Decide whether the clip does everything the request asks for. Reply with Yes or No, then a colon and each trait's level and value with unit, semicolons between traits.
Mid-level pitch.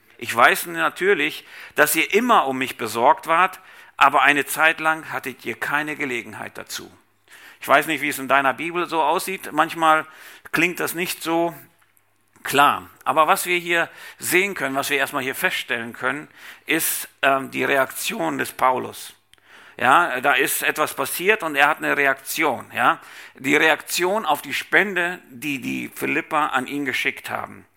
Yes: medium, 155 Hz